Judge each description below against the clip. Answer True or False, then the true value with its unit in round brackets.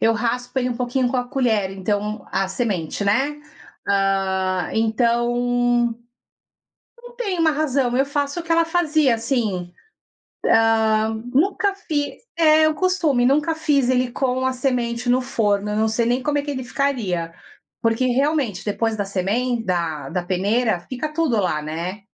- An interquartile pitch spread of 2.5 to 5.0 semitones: False (5.4 semitones)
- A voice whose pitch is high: True (245 Hz)